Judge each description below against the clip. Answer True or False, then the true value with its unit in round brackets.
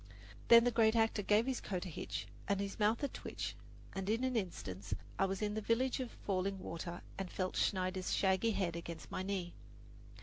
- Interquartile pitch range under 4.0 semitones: True (3.3 semitones)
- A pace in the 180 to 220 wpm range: True (200 wpm)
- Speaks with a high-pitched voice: True (200 Hz)